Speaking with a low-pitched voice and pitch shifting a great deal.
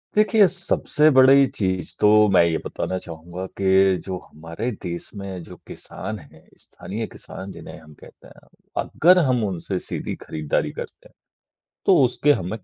Yes: very low, 95 Hz; wide, 7.1 semitones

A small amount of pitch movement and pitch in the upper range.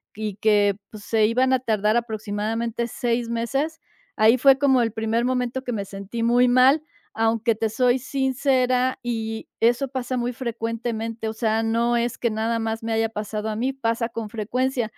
Yes: narrow, 2.1 semitones; high, 230 Hz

